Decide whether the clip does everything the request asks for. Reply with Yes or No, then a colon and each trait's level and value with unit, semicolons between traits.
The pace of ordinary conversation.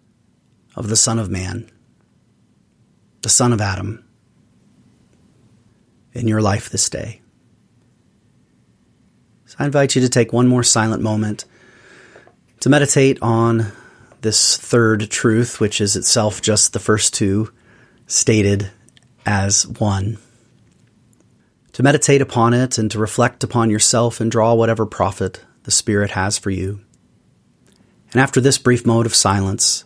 No: slow, 130 wpm